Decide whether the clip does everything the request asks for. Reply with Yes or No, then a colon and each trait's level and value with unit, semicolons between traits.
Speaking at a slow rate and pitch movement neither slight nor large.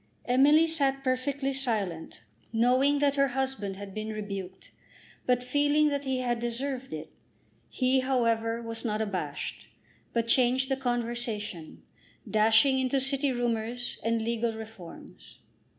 Yes: slow, 130 wpm; average, 3.3 semitones